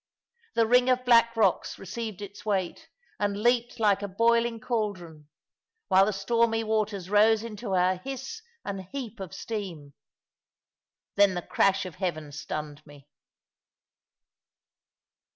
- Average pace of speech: No, slow, 130 wpm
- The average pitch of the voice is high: Yes, high, 205 Hz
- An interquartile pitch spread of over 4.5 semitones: No, average, 3.8 semitones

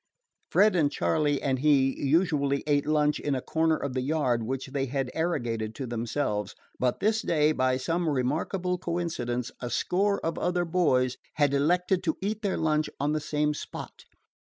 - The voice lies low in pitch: No, medium, 150 Hz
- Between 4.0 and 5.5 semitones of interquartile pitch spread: Yes, average, 4.3 semitones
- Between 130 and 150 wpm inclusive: No, average, 175 wpm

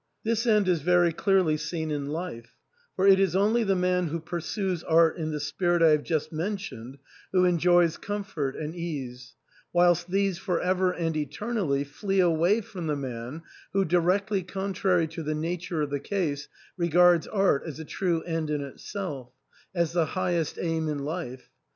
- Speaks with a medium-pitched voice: Yes, medium, 170 Hz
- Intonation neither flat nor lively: Yes, average, 3.4 semitones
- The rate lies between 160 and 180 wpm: Yes, average, 175 wpm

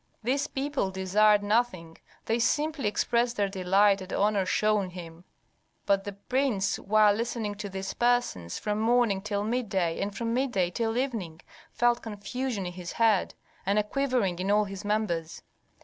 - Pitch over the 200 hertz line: Yes, high, 210 Hz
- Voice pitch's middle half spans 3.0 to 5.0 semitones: Yes, average, 3.6 semitones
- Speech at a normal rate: Yes, average, 160 wpm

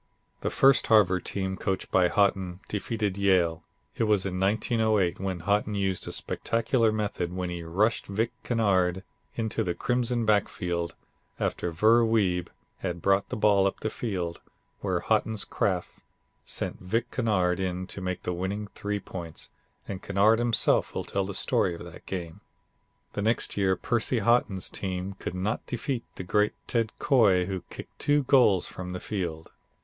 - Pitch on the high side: No, low, 100 Hz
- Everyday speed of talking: Yes, average, 165 wpm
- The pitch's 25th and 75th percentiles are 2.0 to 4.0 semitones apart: Yes, average, 3.3 semitones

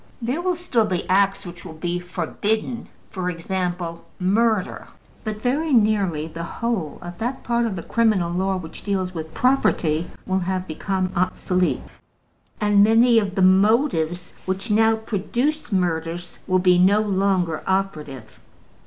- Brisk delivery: No, average, 145 wpm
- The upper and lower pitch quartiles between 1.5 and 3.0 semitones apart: No, average, 3.9 semitones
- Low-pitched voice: No, high, 190 Hz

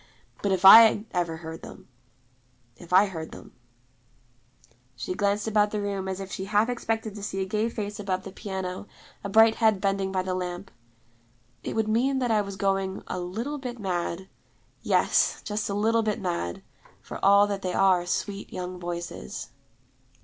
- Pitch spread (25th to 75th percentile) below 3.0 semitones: Yes, narrow, 2.6 semitones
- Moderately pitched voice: No, high, 195 Hz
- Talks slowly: No, average, 180 wpm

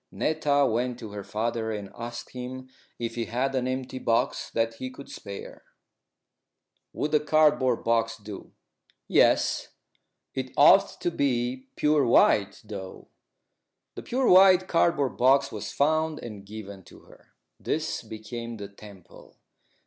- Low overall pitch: Yes, low, 125 Hz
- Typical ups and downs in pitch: Yes, average, 4.3 semitones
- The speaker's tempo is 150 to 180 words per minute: No, average, 140 wpm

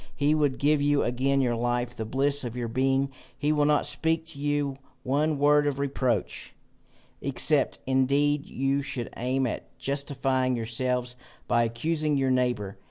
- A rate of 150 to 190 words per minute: Yes, average, 160 wpm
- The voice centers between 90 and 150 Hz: Yes, low, 135 Hz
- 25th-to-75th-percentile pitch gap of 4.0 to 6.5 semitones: No, average, 2.7 semitones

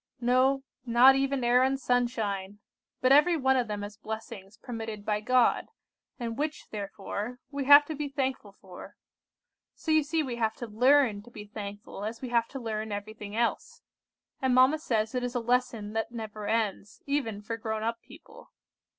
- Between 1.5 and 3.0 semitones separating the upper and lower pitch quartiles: No, average, 3.5 semitones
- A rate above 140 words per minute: Yes, average, 180 wpm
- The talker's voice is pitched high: Yes, high, 235 Hz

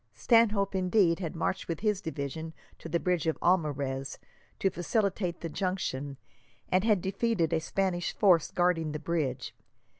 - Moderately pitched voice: Yes, medium, 175 Hz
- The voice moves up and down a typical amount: Yes, average, 3.4 semitones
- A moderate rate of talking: Yes, average, 150 wpm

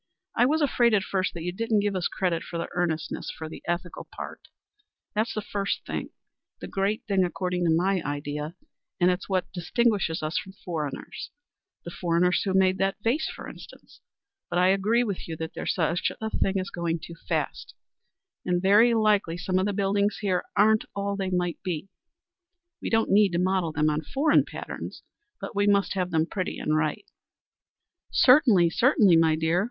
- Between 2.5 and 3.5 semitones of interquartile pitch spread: Yes, average, 3.1 semitones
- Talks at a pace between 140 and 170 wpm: No, average, 185 wpm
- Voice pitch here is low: No, medium, 185 Hz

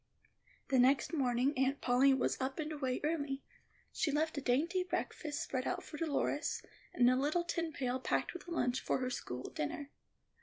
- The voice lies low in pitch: No, very high, 275 Hz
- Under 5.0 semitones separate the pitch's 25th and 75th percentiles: Yes, average, 3.4 semitones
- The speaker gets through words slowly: No, average, 185 wpm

